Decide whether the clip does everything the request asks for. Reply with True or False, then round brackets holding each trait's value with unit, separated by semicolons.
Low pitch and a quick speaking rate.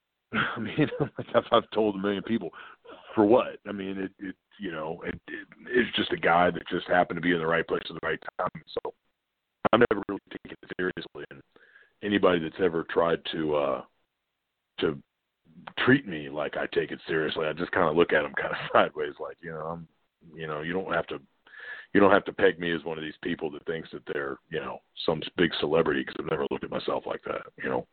True (95 Hz; 230 wpm)